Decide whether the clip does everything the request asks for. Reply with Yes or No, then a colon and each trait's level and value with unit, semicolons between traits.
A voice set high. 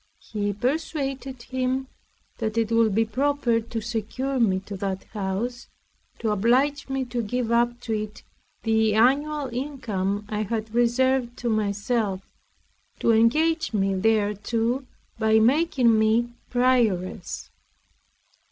Yes: high, 230 Hz